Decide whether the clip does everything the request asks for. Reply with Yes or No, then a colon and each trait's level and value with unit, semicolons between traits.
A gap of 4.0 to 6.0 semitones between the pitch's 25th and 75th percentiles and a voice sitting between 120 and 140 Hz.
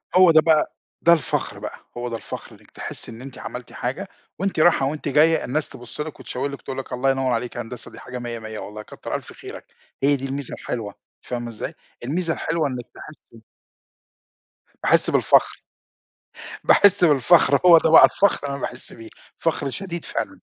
Yes: average, 4.8 semitones; low, 135 Hz